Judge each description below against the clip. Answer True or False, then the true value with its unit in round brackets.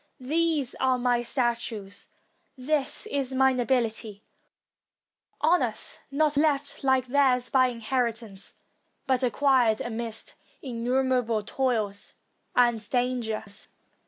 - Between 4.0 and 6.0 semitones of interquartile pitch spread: False (2.5 semitones)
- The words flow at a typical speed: False (95 wpm)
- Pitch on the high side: True (250 Hz)